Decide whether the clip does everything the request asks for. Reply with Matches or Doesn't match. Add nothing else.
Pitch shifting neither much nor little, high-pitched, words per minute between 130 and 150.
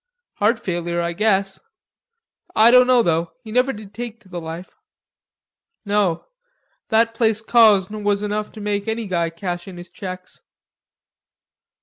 Matches